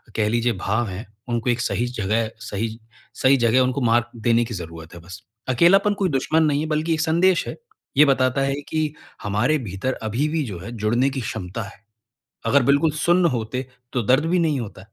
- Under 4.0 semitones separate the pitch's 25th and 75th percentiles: No, average, 5.2 semitones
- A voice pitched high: No, low, 125 Hz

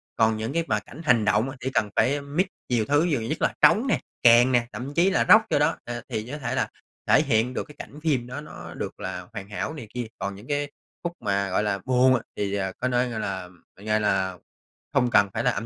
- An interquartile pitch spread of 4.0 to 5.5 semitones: Yes, average, 5.2 semitones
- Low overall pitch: Yes, low, 120 Hz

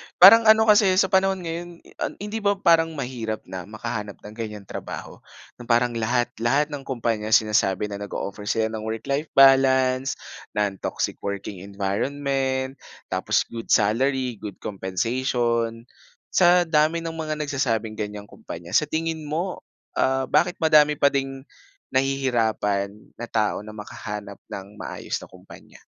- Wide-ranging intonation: Yes, wide, 6.1 semitones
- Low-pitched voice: Yes, low, 130 Hz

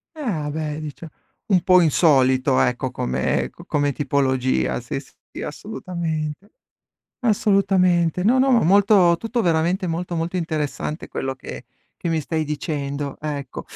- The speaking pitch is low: No, medium, 160 Hz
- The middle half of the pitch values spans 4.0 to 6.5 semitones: Yes, average, 4.4 semitones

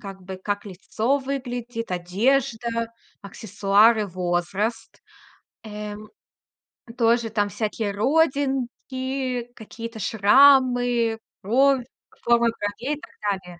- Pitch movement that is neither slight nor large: Yes, average, 3.4 semitones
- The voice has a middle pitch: No, high, 230 Hz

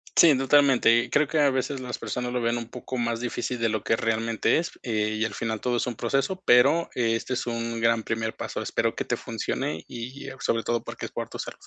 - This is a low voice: Yes, low, 120 Hz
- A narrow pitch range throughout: Yes, narrow, 2.3 semitones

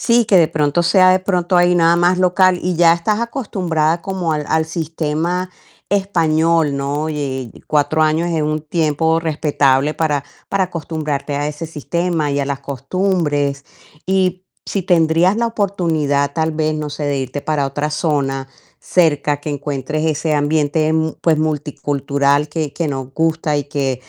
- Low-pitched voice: No, medium, 155 Hz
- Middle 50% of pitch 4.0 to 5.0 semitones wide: No, average, 3.0 semitones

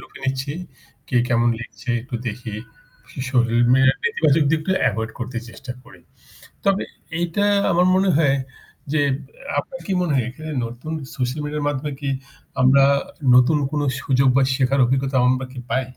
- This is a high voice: No, low, 135 Hz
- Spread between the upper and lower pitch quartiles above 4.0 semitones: No, average, 3.2 semitones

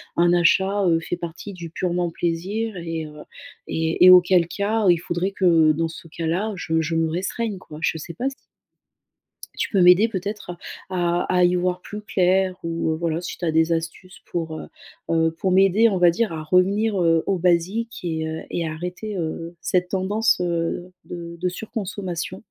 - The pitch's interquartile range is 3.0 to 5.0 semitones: No, narrow, 2.4 semitones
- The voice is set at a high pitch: No, medium, 175 Hz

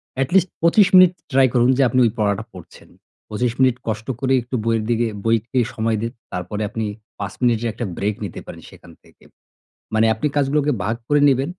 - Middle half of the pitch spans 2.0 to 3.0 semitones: No, average, 3.5 semitones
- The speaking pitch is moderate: No, low, 120 Hz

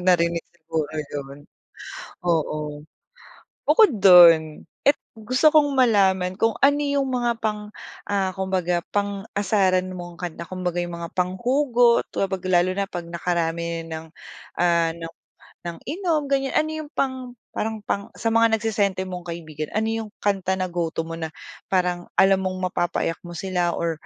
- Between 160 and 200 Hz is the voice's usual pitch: Yes, medium, 185 Hz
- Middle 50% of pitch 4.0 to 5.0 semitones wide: Yes, average, 4.6 semitones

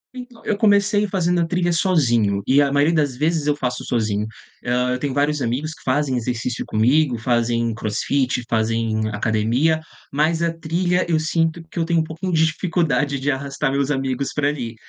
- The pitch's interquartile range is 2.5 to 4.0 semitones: No, average, 5.2 semitones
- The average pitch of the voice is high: No, medium, 145 Hz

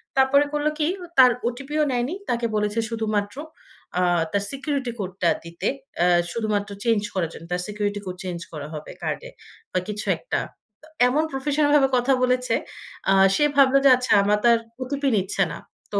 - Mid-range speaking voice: No, high, 235 Hz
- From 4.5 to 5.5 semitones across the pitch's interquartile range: Yes, average, 5.1 semitones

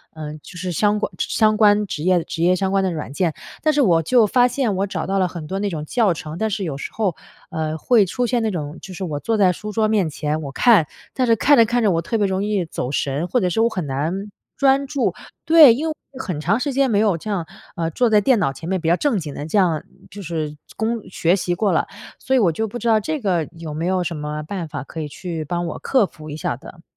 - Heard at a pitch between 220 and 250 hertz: No, high, 190 Hz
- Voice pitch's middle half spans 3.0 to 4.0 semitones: No, average, 5.3 semitones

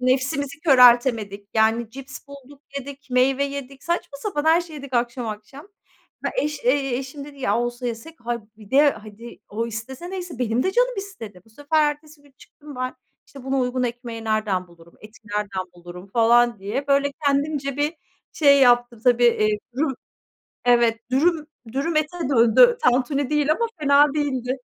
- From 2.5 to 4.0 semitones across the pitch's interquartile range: Yes, average, 3.7 semitones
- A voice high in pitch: Yes, very high, 260 Hz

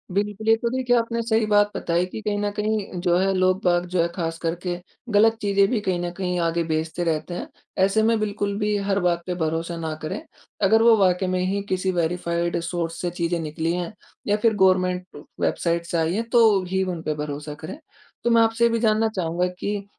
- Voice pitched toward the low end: No, medium, 185 Hz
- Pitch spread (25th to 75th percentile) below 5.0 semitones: Yes, average, 3.5 semitones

